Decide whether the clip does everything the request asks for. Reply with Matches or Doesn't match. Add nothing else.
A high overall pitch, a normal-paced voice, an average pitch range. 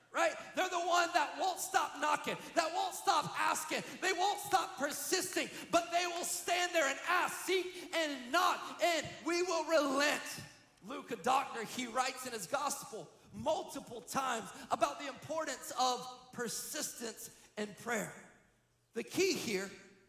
Doesn't match